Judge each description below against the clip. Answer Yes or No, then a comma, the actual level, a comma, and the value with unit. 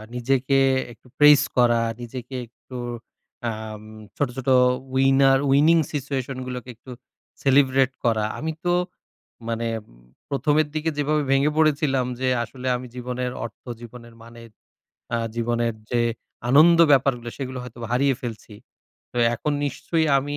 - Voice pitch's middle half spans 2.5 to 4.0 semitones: Yes, average, 2.9 semitones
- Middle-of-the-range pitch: No, low, 130 Hz